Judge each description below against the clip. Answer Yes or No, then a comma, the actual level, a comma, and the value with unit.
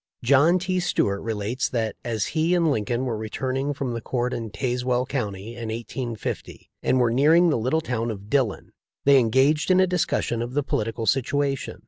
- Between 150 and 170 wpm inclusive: No, average, 190 wpm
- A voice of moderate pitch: No, low, 125 Hz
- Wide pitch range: No, average, 3.8 semitones